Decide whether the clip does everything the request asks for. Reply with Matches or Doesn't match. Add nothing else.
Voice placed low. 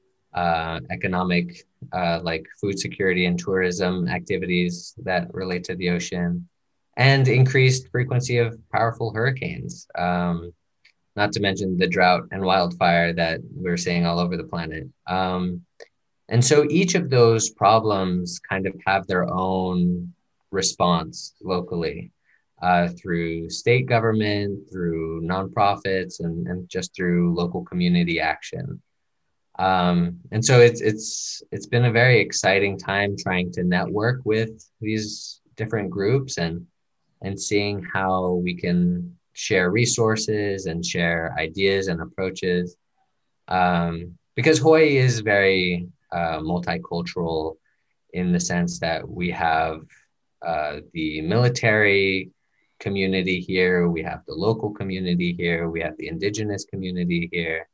Matches